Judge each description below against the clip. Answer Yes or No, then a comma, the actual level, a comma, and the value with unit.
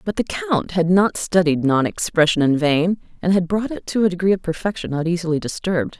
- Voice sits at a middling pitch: Yes, medium, 180 Hz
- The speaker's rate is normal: No, fast, 220 wpm